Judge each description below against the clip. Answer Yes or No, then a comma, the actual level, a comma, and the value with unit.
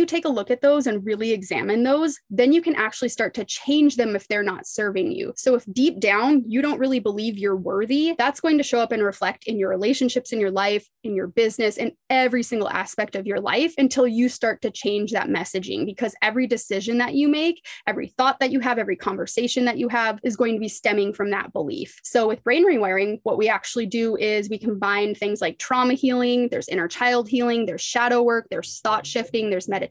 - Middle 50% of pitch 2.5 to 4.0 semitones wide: Yes, average, 3.6 semitones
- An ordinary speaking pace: No, fast, 230 wpm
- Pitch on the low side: No, high, 230 Hz